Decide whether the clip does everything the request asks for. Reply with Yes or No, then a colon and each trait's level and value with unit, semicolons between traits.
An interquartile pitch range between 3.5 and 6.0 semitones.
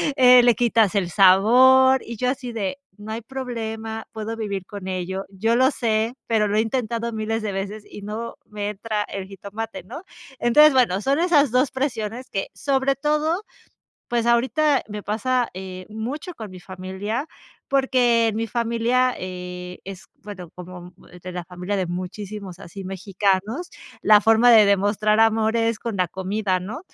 Yes: average, 4.0 semitones